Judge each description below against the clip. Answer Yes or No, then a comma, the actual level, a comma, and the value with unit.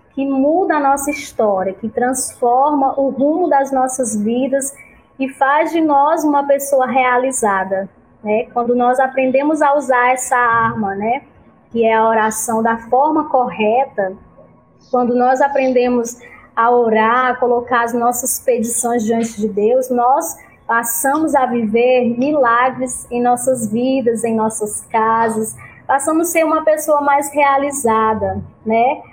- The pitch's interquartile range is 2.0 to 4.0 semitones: Yes, average, 3.1 semitones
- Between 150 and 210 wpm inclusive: No, average, 140 wpm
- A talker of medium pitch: No, very high, 250 Hz